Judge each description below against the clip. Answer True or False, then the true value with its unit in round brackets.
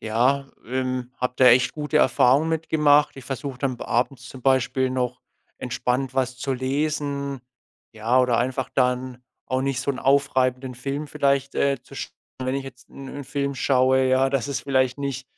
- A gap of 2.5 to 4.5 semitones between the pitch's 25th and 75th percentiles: False (1.5 semitones)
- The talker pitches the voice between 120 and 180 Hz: True (130 Hz)